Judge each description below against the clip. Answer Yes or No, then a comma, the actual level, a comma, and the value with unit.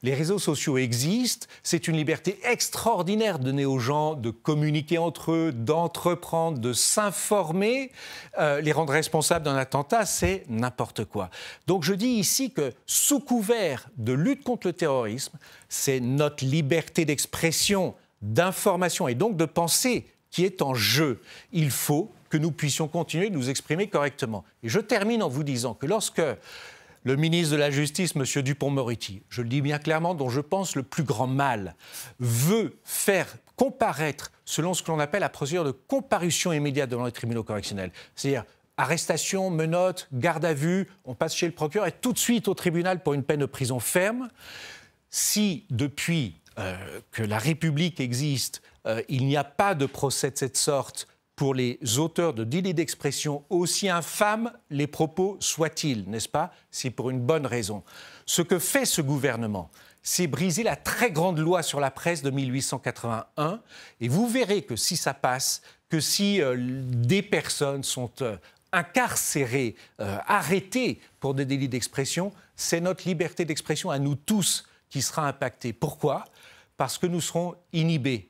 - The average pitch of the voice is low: No, medium, 155 Hz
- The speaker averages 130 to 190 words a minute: Yes, average, 170 wpm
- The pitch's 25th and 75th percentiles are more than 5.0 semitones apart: Yes, wide, 5.4 semitones